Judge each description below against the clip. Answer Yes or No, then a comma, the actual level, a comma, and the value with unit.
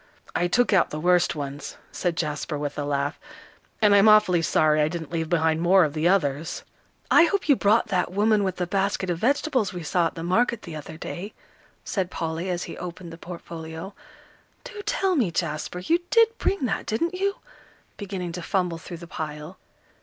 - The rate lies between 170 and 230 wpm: Yes, average, 195 wpm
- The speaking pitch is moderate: Yes, medium, 175 Hz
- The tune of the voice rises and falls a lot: No, average, 4.2 semitones